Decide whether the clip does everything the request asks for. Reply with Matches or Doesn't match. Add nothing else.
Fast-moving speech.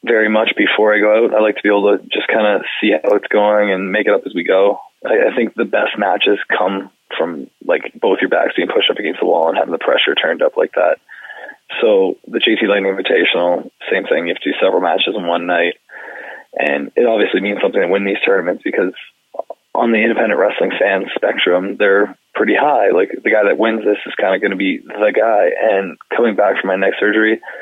Matches